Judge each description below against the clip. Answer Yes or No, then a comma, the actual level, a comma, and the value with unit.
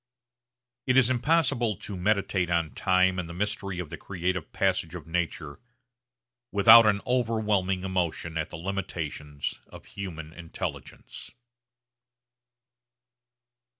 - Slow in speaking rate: Yes, slow, 115 wpm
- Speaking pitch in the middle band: No, very low, 95 Hz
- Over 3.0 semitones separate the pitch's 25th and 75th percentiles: Yes, average, 3.6 semitones